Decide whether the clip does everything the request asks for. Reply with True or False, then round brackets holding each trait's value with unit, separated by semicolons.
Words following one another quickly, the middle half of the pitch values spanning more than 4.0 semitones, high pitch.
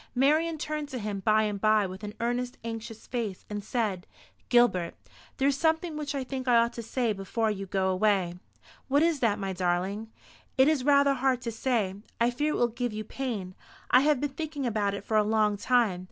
True (220 wpm; 4.5 semitones; 230 Hz)